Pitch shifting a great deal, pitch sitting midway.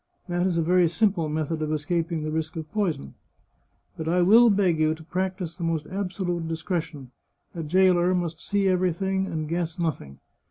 No: average, 2.7 semitones; medium, 170 Hz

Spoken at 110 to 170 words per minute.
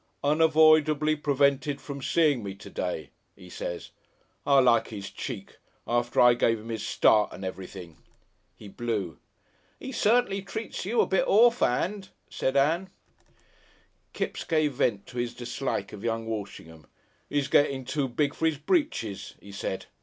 Yes: average, 150 wpm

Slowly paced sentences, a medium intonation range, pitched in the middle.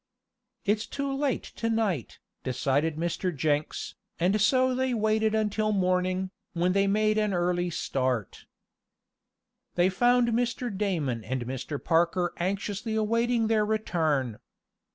No: slow, 125 wpm; average, 4.9 semitones; high, 195 Hz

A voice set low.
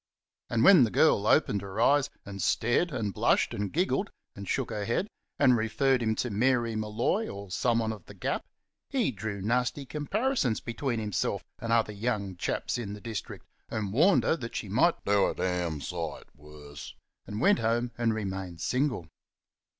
Yes: low, 110 Hz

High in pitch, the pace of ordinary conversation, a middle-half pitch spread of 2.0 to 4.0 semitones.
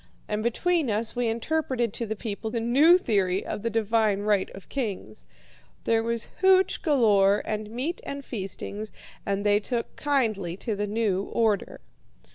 Yes: high, 225 Hz; average, 160 wpm; average, 3.1 semitones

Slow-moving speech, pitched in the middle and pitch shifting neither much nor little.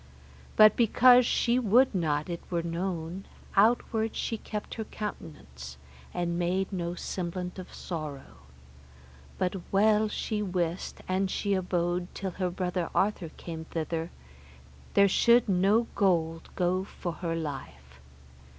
Yes: slow, 130 wpm; medium, 180 Hz; average, 3.4 semitones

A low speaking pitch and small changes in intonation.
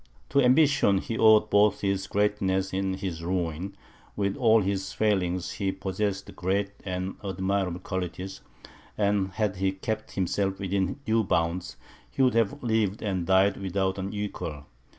Yes: very low, 95 Hz; narrow, 1.6 semitones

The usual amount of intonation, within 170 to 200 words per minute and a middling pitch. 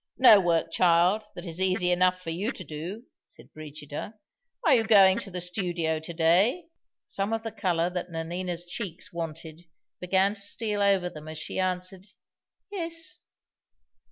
No: average, 3.2 semitones; average, 160 wpm; medium, 180 Hz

